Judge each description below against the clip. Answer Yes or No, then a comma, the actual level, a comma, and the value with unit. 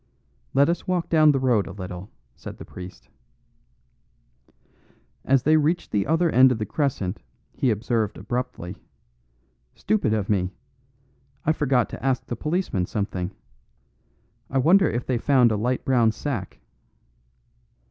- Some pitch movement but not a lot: No, wide, 5.8 semitones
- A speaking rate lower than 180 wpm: Yes, average, 140 wpm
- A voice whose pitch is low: Yes, low, 125 Hz